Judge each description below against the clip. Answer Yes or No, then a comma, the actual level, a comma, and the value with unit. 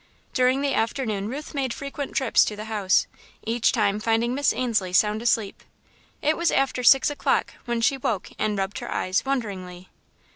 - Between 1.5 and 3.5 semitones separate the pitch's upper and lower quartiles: No, average, 4.4 semitones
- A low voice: No, high, 230 Hz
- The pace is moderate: Yes, average, 175 wpm